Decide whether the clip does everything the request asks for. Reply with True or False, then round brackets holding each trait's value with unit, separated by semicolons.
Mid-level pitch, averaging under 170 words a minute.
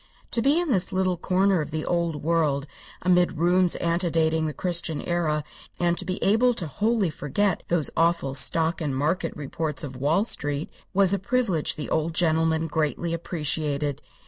True (165 Hz; 160 wpm)